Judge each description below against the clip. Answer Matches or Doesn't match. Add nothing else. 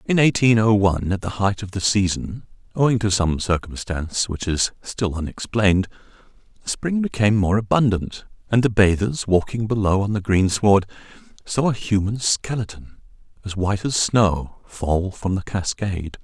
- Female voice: Doesn't match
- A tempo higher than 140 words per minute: Matches